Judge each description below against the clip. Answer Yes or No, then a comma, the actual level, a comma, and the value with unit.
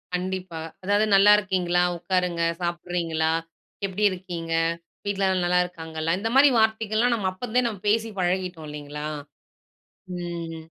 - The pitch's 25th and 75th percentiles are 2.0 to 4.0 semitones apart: Yes, average, 3.1 semitones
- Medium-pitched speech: Yes, medium, 180 Hz